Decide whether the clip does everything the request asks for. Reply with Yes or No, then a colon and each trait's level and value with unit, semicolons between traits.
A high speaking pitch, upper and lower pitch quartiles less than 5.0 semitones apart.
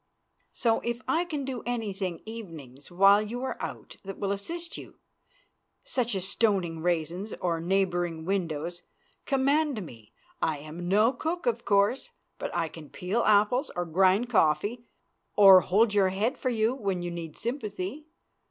No: high, 200 Hz; average, 5.3 semitones